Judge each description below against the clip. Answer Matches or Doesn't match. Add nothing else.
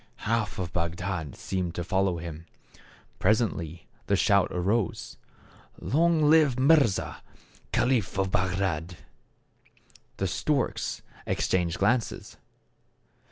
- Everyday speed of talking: Doesn't match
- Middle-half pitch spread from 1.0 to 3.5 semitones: Doesn't match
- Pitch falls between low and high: Doesn't match